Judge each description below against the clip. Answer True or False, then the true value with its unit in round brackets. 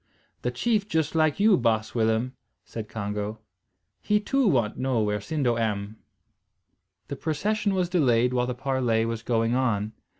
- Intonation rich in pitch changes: True (6.0 semitones)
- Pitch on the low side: True (125 Hz)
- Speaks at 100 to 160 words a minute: True (155 wpm)